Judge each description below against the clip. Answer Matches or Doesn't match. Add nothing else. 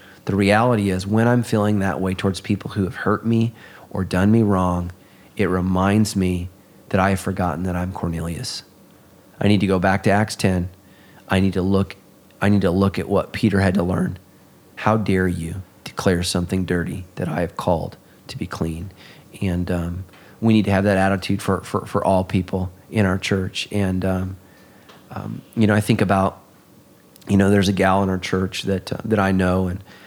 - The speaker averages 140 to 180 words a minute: Doesn't match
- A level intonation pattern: Matches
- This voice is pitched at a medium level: Doesn't match